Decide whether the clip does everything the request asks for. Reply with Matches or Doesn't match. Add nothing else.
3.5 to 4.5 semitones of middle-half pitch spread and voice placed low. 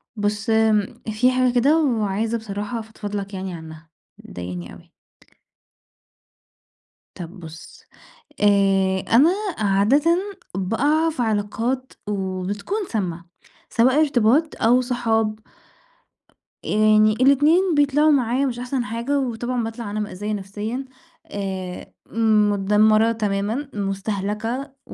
Doesn't match